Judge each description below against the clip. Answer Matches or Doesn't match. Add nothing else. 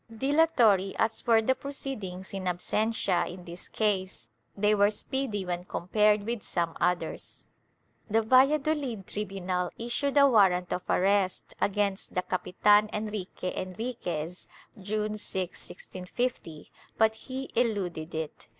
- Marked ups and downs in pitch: Doesn't match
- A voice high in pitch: Matches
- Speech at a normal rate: Doesn't match